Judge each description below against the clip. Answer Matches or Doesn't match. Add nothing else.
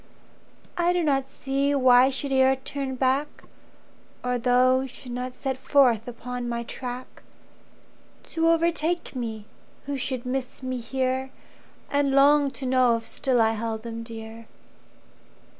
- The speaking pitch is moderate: Doesn't match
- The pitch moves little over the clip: Matches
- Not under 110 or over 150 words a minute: Matches